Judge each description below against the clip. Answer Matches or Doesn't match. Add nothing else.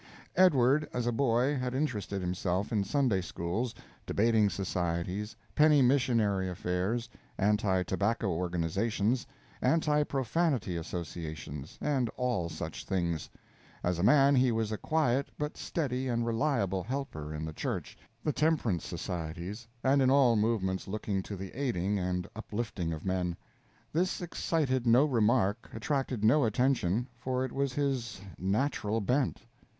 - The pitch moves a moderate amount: Doesn't match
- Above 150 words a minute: Doesn't match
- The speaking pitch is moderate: Doesn't match